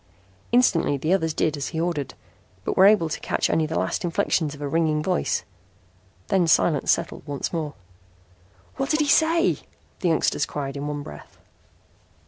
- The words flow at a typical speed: Yes, average, 170 wpm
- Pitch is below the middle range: No, medium, 160 Hz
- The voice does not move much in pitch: No, average, 4.1 semitones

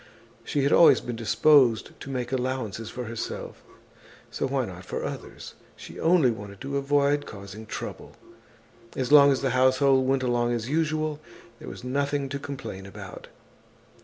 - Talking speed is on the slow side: No, average, 160 wpm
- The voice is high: No, low, 130 Hz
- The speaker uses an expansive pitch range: No, average, 3.3 semitones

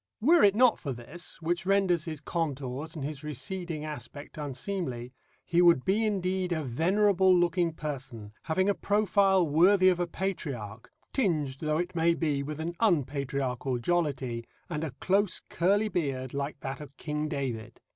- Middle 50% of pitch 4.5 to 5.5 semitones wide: Yes, average, 5.1 semitones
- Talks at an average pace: Yes, average, 160 wpm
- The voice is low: No, medium, 160 Hz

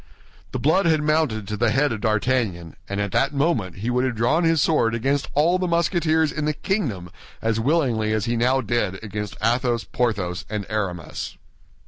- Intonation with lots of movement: Yes, wide, 6.0 semitones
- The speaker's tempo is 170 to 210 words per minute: Yes, average, 185 wpm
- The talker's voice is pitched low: Yes, low, 120 Hz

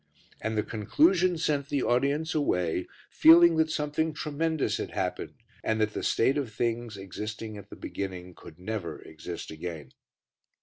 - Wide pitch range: Yes, wide, 7.6 semitones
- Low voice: Yes, low, 115 Hz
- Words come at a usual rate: Yes, average, 150 wpm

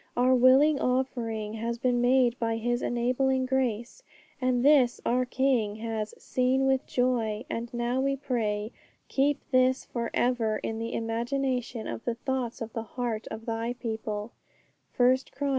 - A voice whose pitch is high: Yes, high, 245 Hz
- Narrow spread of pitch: Yes, narrow, 2.3 semitones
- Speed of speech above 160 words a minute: No, average, 155 wpm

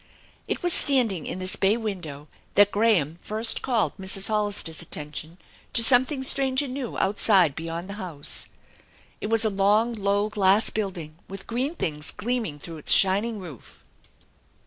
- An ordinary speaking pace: Yes, average, 155 wpm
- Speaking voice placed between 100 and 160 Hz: No, high, 200 Hz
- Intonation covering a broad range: No, average, 4.9 semitones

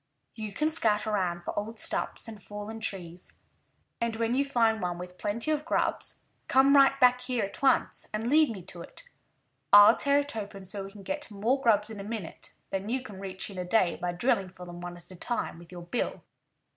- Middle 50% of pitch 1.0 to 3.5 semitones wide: No, average, 4.7 semitones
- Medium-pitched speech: No, high, 210 Hz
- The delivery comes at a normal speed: No, fast, 220 wpm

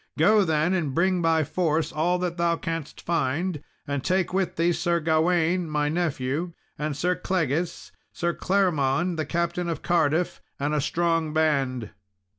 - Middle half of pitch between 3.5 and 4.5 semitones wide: No, narrow, 2.6 semitones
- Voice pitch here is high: No, medium, 165 Hz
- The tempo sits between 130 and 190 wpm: Yes, average, 155 wpm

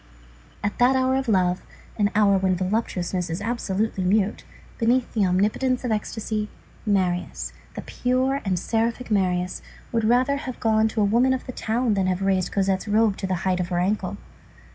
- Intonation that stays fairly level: No, average, 4.0 semitones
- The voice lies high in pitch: Yes, high, 210 Hz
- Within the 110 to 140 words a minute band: No, average, 180 wpm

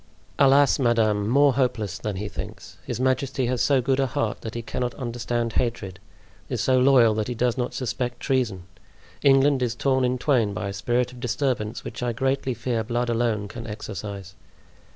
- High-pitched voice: No, low, 120 Hz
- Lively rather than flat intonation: No, average, 2.9 semitones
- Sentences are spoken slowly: No, average, 185 wpm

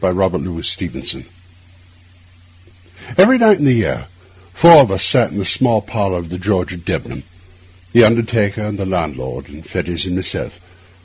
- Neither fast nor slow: Yes, average, 160 wpm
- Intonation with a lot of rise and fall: No, average, 4.0 semitones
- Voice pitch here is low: Yes, very low, 95 Hz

